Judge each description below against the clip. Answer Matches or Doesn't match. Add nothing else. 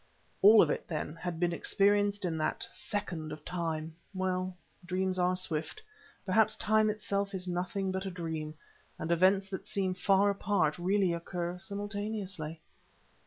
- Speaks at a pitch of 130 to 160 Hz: Doesn't match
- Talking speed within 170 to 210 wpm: Doesn't match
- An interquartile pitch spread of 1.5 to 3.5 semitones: Matches